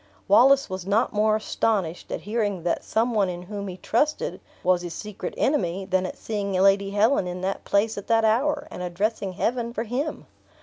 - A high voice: Yes, high, 205 Hz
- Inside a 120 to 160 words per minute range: No, average, 190 wpm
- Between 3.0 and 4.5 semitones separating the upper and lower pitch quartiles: Yes, average, 3.4 semitones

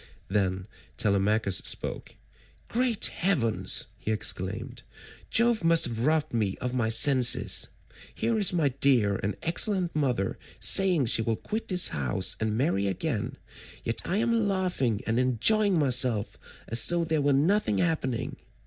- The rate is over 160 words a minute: No, average, 140 wpm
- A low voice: Yes, low, 130 Hz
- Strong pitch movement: Yes, wide, 8.5 semitones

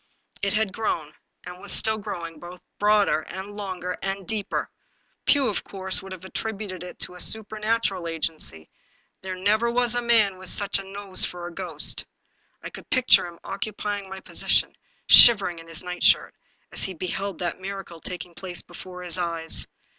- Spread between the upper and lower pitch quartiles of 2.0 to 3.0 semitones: Yes, average, 2.7 semitones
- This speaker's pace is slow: No, average, 170 wpm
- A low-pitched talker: No, high, 190 Hz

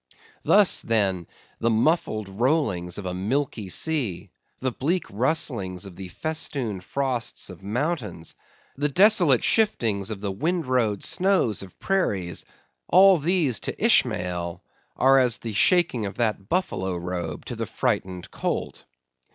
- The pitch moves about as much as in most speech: No, wide, 8.3 semitones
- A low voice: Yes, low, 115 Hz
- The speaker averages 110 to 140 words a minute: Yes, slow, 135 wpm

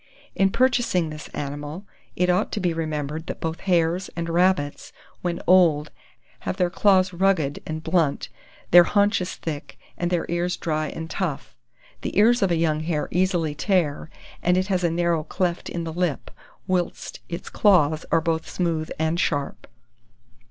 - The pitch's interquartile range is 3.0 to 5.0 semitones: No, narrow, 2.6 semitones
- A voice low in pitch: No, medium, 170 Hz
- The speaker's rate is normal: Yes, average, 165 wpm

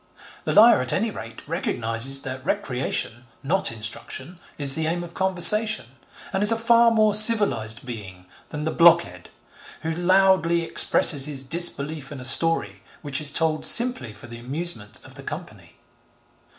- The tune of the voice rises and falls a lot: Yes, wide, 7.1 semitones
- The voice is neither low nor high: Yes, medium, 155 Hz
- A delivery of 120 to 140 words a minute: No, average, 155 wpm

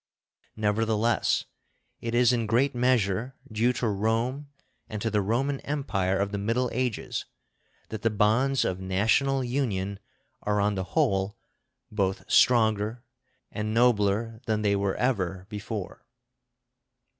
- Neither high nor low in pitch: No, low, 110 Hz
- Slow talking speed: Yes, slow, 130 wpm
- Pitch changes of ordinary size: Yes, average, 3.4 semitones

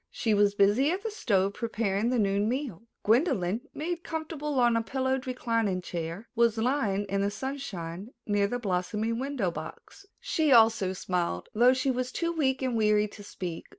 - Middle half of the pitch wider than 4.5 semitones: Yes, average, 4.9 semitones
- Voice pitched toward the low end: No, high, 225 Hz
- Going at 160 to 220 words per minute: Yes, average, 175 wpm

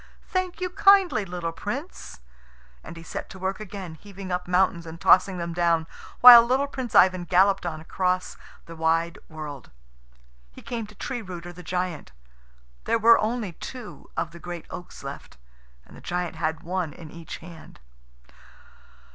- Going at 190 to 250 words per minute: No, average, 165 wpm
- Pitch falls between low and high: Yes, medium, 180 Hz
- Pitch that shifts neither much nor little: Yes, average, 4.1 semitones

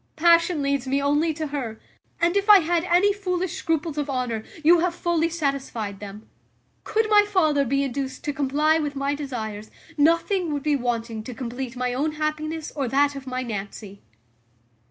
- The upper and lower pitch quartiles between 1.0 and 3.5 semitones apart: No, average, 4.6 semitones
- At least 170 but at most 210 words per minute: Yes, average, 175 wpm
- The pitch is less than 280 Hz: No, very high, 285 Hz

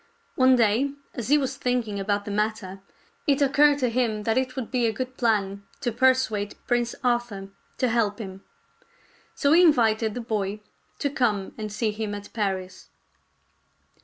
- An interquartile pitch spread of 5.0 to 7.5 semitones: No, average, 3.8 semitones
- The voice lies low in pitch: No, high, 225 Hz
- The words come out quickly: No, average, 165 wpm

